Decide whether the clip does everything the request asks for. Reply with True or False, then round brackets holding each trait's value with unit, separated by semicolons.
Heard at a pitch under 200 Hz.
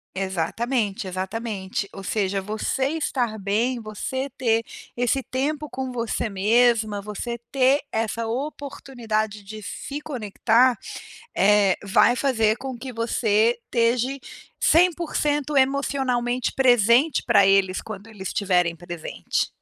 False (230 Hz)